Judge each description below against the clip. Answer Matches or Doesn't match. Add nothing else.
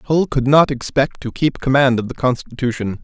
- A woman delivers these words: Doesn't match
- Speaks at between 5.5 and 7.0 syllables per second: Doesn't match